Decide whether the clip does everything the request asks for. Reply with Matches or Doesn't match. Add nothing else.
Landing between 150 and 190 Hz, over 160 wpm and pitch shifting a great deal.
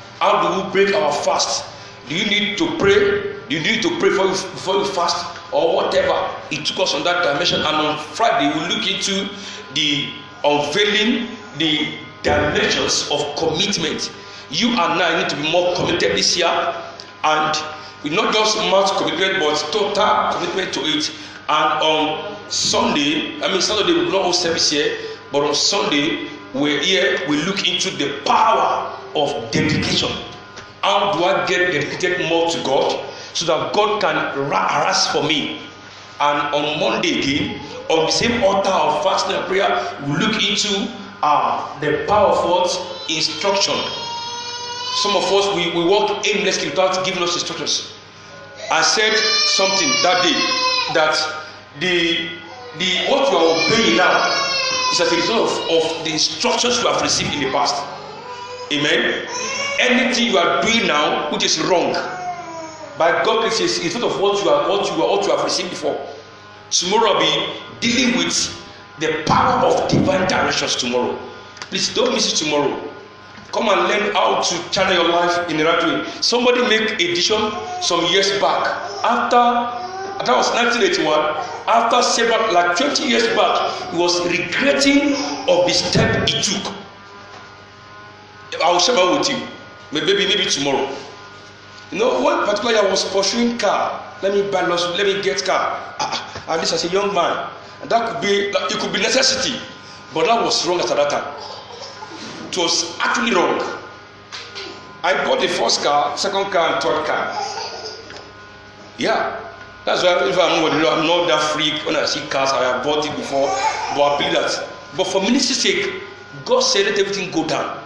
Matches